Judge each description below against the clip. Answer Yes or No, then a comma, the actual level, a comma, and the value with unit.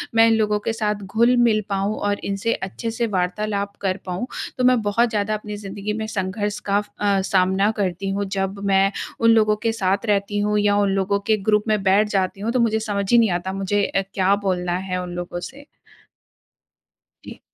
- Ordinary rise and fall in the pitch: No, narrow, 1.9 semitones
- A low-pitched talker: No, high, 205 Hz